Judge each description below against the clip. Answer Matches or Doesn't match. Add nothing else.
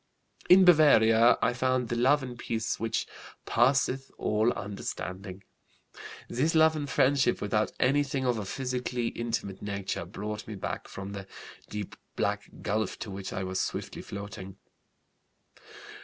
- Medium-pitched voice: Doesn't match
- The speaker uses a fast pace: Doesn't match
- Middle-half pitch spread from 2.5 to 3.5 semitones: Doesn't match